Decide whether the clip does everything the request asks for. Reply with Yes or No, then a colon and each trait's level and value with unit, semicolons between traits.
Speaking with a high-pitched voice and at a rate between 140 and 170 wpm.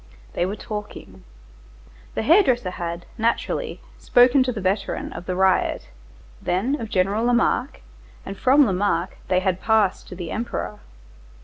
Yes: high, 205 Hz; average, 145 wpm